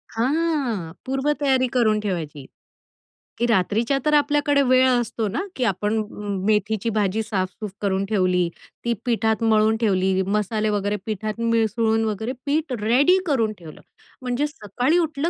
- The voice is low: No, high, 225 Hz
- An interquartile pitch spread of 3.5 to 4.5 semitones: Yes, average, 4.0 semitones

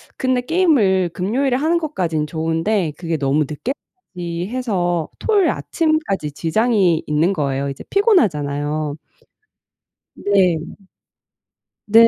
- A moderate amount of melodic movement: No, wide, 8.3 semitones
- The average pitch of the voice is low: No, medium, 185 Hz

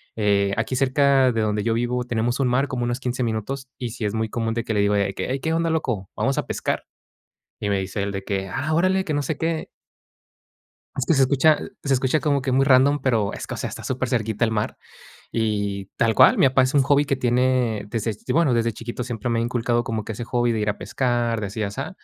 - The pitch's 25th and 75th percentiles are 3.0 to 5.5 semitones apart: Yes, average, 3.5 semitones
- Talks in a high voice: No, low, 120 Hz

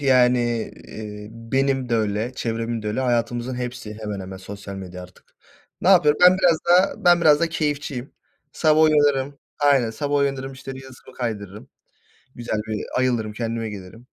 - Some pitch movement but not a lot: Yes, average, 4.5 semitones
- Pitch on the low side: Yes, low, 125 Hz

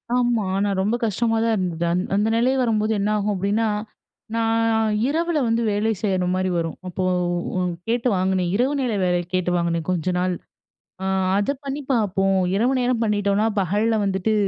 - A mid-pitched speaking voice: No, high, 210 Hz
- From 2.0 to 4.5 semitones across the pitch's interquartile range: Yes, average, 3.6 semitones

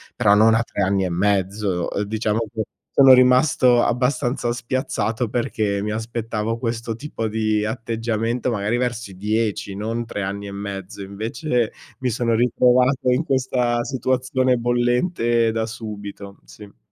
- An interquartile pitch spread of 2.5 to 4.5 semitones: Yes, average, 2.8 semitones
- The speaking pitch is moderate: No, low, 115 Hz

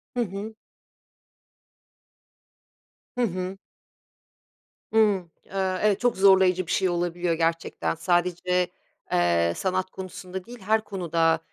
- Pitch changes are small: Yes, narrow, 2.1 semitones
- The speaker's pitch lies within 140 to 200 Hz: Yes, medium, 185 Hz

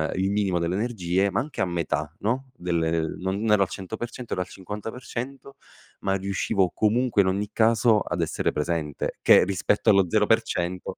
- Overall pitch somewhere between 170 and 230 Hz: No, low, 100 Hz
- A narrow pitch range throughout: No, average, 3.9 semitones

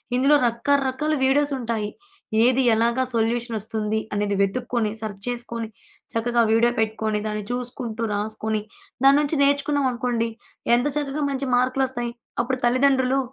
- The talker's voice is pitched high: Yes, high, 240 Hz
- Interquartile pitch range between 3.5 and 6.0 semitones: No, average, 3.1 semitones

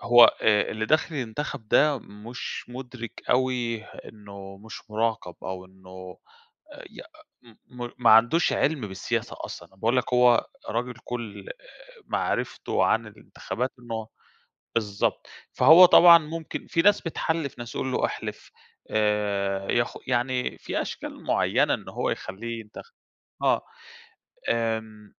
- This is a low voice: Yes, low, 115 Hz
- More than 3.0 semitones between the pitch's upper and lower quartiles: Yes, average, 3.4 semitones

